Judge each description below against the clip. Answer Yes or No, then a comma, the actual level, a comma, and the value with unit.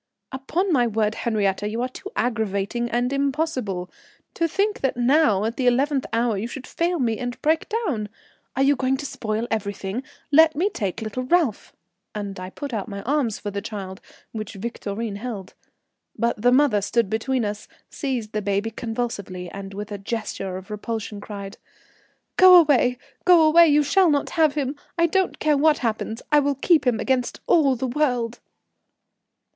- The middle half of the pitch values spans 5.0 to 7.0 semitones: Yes, average, 5.3 semitones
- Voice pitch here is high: Yes, high, 240 Hz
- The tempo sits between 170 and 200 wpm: Yes, average, 175 wpm